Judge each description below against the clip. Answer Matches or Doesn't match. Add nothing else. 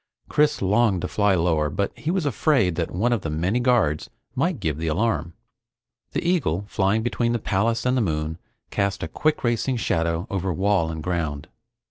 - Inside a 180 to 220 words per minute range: Matches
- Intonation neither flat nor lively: Doesn't match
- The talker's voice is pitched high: Doesn't match